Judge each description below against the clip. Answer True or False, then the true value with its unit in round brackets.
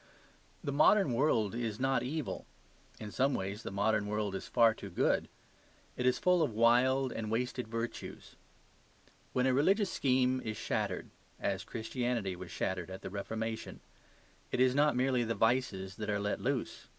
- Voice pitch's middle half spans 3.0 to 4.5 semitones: True (3.9 semitones)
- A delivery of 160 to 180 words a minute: True (165 wpm)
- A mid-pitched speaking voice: False (115 Hz)